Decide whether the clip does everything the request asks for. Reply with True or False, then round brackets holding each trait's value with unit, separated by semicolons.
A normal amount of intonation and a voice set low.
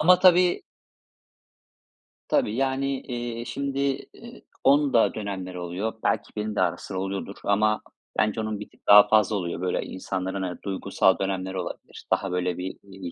True (4.2 semitones; 100 Hz)